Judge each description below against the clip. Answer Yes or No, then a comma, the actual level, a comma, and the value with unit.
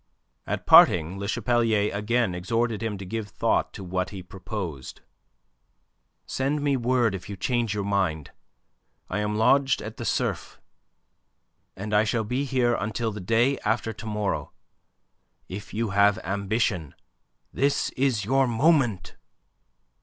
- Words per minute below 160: Yes, average, 140 wpm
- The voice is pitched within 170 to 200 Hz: No, low, 105 Hz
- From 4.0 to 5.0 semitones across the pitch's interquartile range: No, average, 3.4 semitones